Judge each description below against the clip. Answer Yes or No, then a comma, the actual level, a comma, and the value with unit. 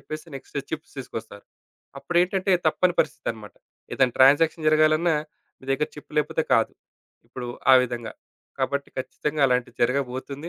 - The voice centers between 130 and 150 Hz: Yes, medium, 140 Hz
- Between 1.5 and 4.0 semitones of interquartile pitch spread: Yes, average, 3.6 semitones